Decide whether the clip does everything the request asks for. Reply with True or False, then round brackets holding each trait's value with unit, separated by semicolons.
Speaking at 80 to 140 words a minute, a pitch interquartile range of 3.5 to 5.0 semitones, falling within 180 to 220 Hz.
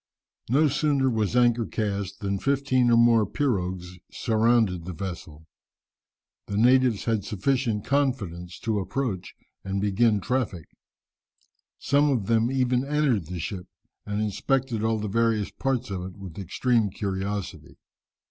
False (135 wpm; 4.5 semitones; 110 Hz)